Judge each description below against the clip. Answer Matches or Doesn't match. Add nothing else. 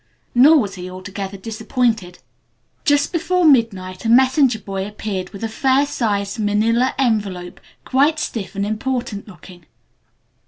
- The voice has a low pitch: Doesn't match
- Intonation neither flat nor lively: Matches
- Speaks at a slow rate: Matches